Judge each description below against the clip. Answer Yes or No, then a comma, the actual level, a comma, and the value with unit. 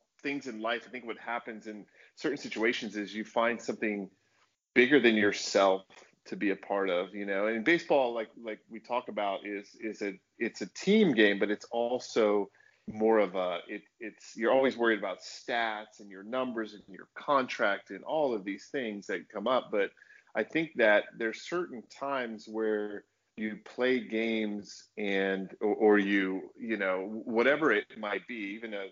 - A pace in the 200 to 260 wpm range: No, average, 185 wpm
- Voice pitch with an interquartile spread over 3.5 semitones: No, narrow, 2.6 semitones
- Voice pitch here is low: Yes, low, 110 Hz